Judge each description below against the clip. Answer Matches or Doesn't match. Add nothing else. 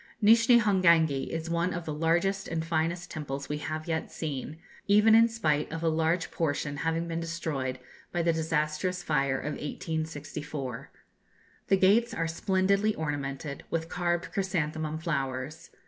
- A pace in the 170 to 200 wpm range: Doesn't match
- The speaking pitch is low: Doesn't match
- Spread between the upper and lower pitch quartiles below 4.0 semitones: Matches